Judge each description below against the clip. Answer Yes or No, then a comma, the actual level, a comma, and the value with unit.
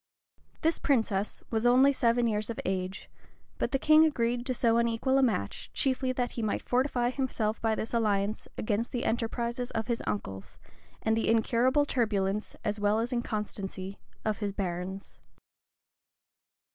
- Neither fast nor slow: Yes, average, 155 wpm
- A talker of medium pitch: No, high, 230 Hz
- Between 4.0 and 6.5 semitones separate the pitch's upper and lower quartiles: No, average, 3.0 semitones